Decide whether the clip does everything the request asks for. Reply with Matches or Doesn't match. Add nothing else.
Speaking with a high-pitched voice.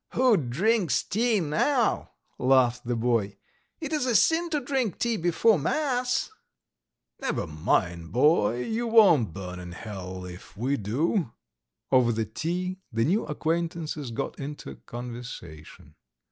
Doesn't match